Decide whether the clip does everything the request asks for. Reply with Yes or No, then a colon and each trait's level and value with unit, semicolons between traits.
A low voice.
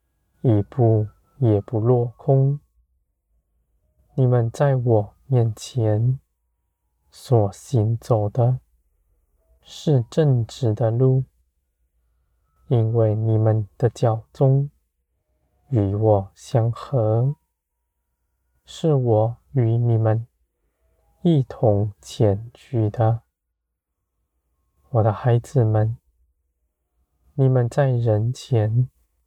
Yes: low, 105 Hz